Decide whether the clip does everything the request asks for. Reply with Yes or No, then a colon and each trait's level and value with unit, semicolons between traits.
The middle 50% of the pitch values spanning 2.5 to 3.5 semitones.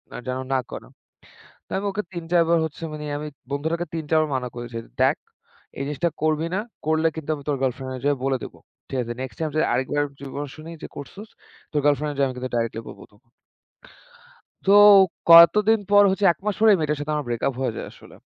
No: average, 4.0 semitones